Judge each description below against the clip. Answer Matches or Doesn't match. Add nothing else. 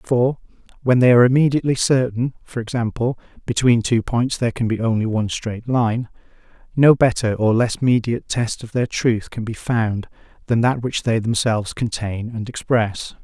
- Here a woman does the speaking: Doesn't match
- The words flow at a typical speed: Matches